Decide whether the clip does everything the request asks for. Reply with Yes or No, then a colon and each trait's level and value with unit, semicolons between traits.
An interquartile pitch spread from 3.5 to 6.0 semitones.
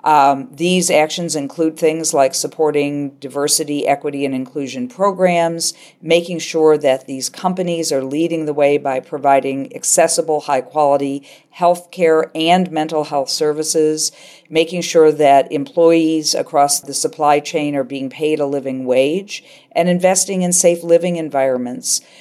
No: average, 3.1 semitones